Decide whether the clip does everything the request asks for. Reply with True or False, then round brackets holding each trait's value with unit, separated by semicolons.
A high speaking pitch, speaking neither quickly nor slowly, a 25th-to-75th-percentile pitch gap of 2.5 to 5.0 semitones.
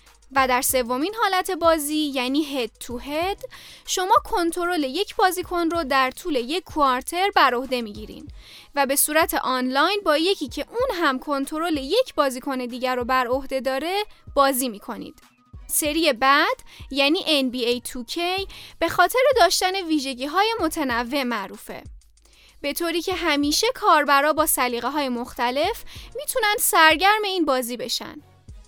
False (295 Hz; 140 wpm; 5.4 semitones)